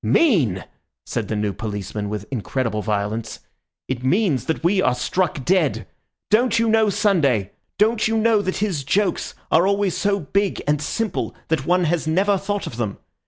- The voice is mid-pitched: Yes, medium, 165 Hz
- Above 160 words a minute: Yes, average, 170 wpm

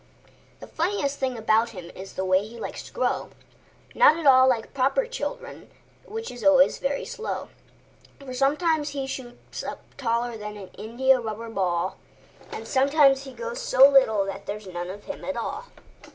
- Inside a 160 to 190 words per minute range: Yes, average, 165 wpm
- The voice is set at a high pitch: Yes, very high, 260 Hz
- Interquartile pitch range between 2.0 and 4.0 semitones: No, average, 4.9 semitones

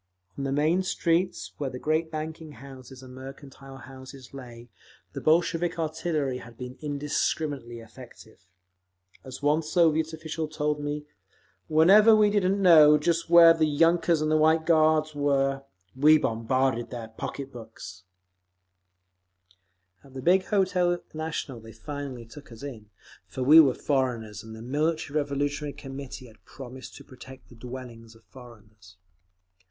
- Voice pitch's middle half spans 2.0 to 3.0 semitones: No, average, 3.8 semitones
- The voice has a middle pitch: Yes, medium, 145 Hz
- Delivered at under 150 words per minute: Yes, average, 140 wpm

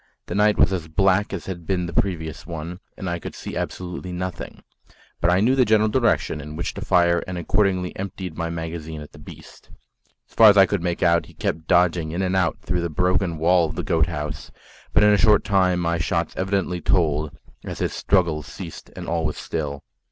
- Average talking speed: No, fast, 220 wpm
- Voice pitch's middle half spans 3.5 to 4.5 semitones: No, average, 2.7 semitones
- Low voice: Yes, very low, 90 Hz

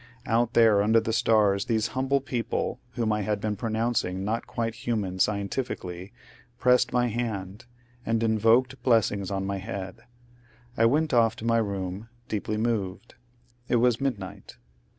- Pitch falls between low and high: No, low, 110 Hz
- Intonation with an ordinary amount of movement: Yes, average, 3.0 semitones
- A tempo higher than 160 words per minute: No, average, 150 wpm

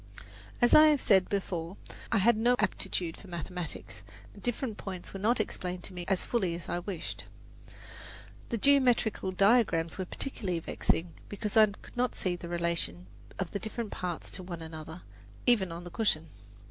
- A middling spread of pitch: Yes, average, 4.3 semitones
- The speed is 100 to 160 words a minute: No, average, 170 wpm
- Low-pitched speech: No, high, 190 Hz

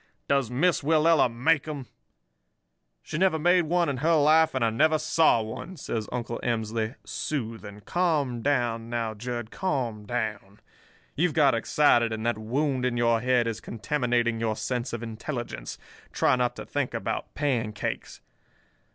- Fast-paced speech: No, average, 150 wpm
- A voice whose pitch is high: No, low, 125 Hz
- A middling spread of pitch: Yes, average, 4.7 semitones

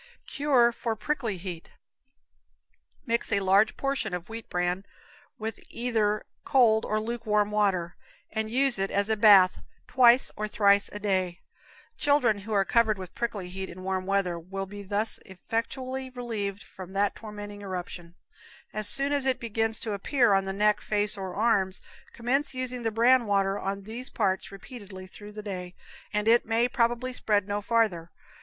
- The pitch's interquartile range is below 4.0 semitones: Yes, average, 3.2 semitones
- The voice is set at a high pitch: Yes, high, 210 Hz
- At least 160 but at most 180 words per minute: Yes, average, 165 wpm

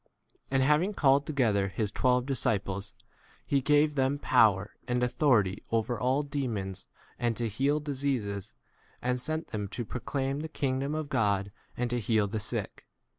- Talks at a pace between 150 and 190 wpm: Yes, average, 170 wpm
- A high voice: No, low, 125 Hz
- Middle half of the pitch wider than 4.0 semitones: Yes, average, 4.9 semitones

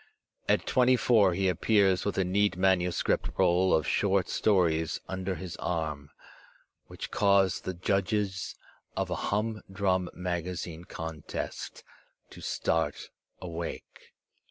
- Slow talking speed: Yes, slow, 115 wpm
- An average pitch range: No, narrow, 2.3 semitones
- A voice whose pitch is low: Yes, very low, 95 Hz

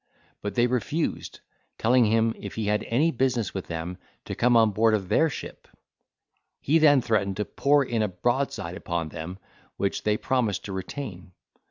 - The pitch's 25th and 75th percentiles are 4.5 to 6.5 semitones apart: Yes, average, 4.8 semitones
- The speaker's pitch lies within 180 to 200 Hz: No, low, 110 Hz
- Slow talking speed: No, average, 175 wpm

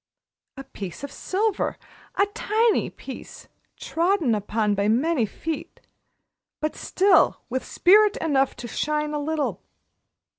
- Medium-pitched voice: No, very high, 300 Hz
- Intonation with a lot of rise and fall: Yes, wide, 7.3 semitones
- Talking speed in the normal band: No, slow, 120 wpm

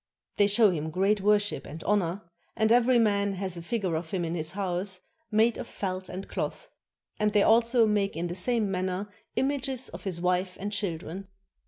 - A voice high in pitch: Yes, high, 195 Hz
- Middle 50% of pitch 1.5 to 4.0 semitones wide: Yes, average, 2.9 semitones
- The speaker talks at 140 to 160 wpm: No, average, 190 wpm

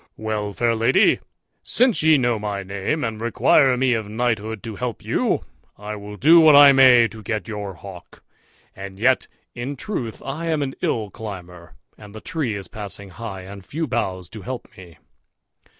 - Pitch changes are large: No, average, 4.4 semitones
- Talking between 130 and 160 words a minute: No, average, 180 wpm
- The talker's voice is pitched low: Yes, low, 110 Hz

